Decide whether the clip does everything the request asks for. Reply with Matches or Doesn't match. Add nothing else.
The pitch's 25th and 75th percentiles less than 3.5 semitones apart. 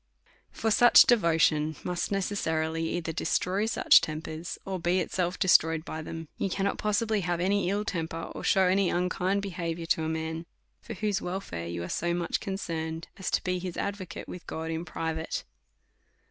Matches